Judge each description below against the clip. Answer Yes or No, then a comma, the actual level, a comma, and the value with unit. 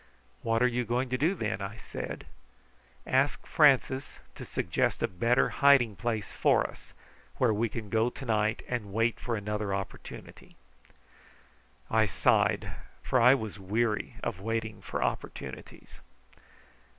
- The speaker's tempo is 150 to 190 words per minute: No, average, 140 wpm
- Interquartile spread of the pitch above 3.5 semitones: No, average, 2.8 semitones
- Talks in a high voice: No, low, 115 Hz